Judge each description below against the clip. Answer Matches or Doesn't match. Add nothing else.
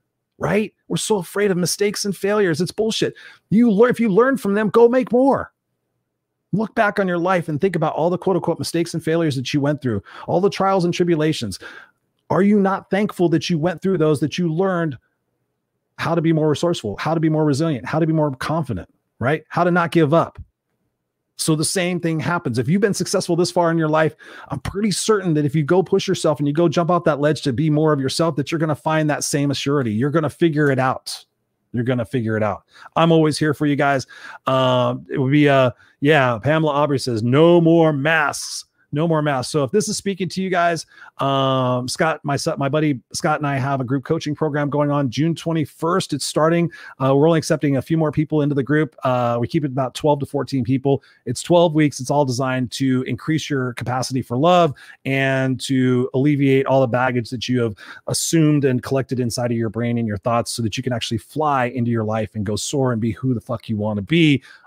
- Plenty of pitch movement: Doesn't match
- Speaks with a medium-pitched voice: Matches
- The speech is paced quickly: Matches